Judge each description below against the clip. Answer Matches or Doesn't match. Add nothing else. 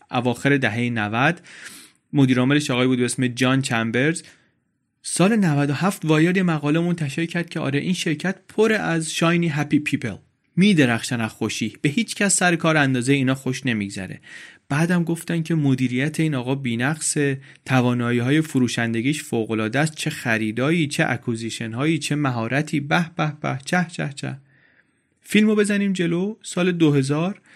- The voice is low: Doesn't match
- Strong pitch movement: Doesn't match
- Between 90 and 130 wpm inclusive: Doesn't match